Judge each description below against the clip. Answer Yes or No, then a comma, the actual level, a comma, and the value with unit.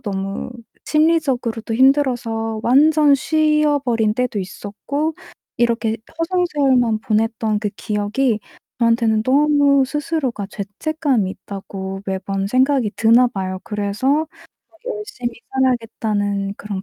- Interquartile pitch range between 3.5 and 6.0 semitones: Yes, wide, 5.5 semitones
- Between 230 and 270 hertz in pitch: Yes, high, 235 Hz